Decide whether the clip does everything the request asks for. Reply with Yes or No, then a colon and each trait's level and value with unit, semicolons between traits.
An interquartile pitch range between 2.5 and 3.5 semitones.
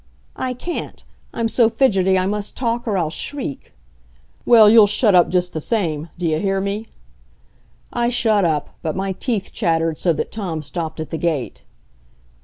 No: average, 5.3 semitones